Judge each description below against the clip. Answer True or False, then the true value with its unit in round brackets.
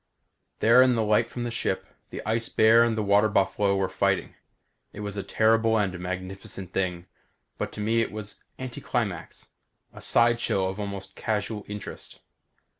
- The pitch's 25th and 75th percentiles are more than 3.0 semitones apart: False (2.7 semitones)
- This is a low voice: True (105 Hz)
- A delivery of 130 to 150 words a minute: False (165 wpm)